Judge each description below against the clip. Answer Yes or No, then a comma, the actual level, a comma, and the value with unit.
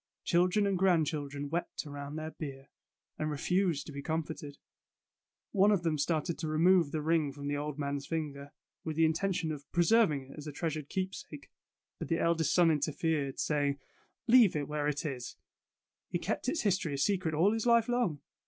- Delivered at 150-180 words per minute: No, average, 195 wpm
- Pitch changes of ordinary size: Yes, average, 3.6 semitones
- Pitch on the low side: No, medium, 155 Hz